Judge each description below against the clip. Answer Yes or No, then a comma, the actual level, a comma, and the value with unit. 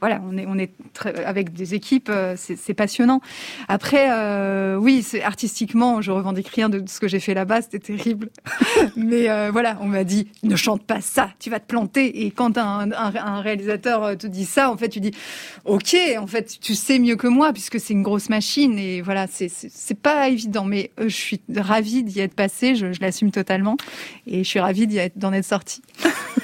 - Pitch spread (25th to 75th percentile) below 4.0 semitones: Yes, average, 3.1 semitones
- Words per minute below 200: No, fast, 220 wpm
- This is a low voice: No, high, 210 Hz